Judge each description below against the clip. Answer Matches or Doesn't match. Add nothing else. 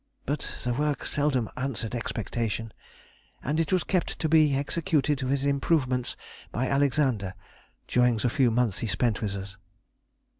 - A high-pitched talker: Doesn't match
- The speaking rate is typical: Matches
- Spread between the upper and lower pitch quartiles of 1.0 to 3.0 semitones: Doesn't match